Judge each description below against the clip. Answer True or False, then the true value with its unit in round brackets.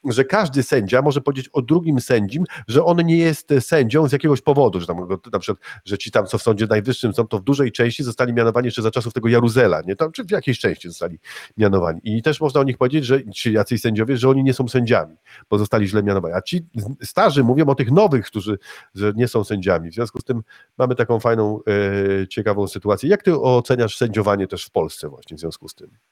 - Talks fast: True (230 wpm)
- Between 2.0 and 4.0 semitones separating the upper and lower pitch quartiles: False (4.7 semitones)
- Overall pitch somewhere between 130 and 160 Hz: False (120 Hz)